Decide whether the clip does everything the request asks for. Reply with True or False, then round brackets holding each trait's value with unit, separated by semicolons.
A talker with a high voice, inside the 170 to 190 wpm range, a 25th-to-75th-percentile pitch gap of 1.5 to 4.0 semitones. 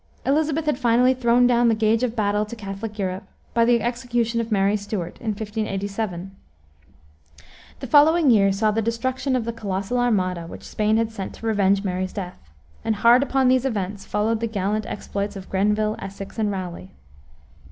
True (215 Hz; 175 wpm; 3.2 semitones)